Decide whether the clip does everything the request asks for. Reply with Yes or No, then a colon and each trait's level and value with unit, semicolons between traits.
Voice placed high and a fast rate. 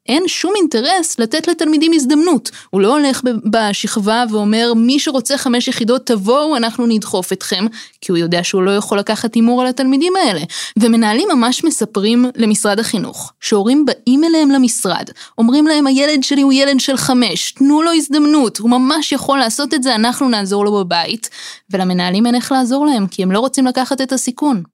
Yes: high, 245 Hz; fast, 175 wpm